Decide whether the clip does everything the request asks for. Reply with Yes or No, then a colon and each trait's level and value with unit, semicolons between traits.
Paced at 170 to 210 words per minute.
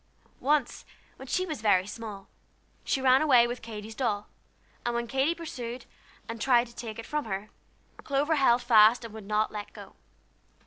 Yes: average, 175 wpm